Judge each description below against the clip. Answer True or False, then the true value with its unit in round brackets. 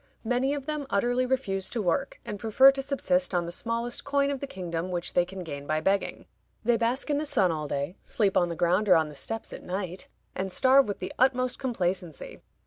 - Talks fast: True (225 wpm)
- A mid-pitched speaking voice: False (200 Hz)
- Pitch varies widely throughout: True (6.2 semitones)